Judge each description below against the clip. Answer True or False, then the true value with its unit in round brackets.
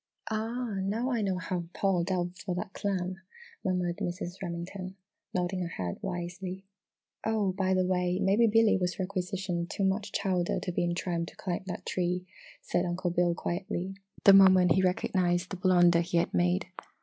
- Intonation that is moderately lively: False (1.7 semitones)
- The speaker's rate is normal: True (175 wpm)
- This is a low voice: False (185 Hz)